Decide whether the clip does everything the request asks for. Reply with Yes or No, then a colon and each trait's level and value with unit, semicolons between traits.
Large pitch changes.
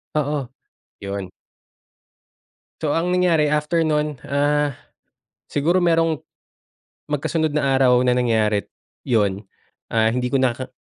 No: average, 3.8 semitones